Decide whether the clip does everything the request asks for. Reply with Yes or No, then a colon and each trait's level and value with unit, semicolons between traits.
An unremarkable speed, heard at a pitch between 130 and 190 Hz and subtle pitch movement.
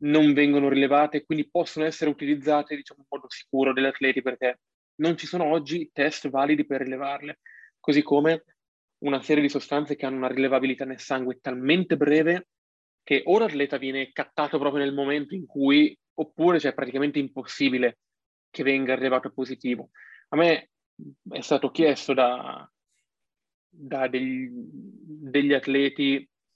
Yes: average, 150 wpm; medium, 140 Hz; narrow, 2.2 semitones